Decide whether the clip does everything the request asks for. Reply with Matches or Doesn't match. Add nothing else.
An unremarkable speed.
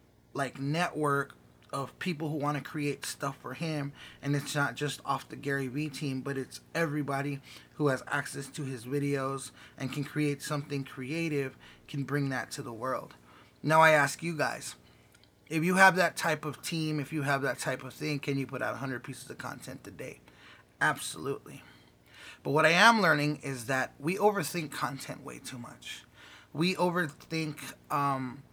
Matches